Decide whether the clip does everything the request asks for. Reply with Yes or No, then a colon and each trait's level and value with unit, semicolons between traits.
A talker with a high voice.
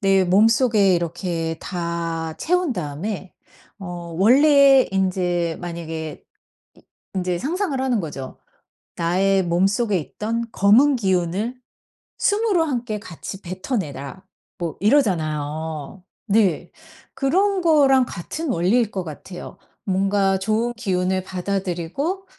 Yes: high, 195 Hz